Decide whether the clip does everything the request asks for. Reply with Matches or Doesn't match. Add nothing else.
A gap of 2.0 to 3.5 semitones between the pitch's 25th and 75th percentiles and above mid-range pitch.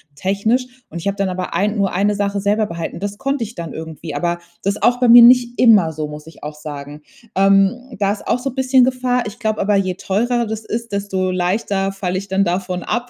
Doesn't match